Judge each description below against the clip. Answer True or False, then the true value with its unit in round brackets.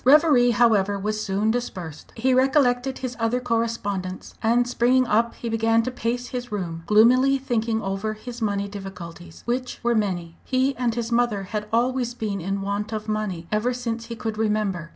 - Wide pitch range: False (3.3 semitones)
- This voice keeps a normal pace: True (175 wpm)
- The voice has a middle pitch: False (225 Hz)